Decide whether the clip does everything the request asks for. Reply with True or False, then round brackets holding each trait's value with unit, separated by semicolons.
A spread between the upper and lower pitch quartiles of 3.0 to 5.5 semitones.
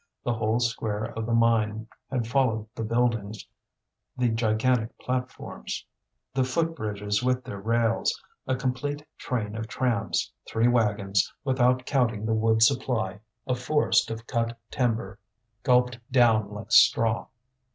False (2.4 semitones)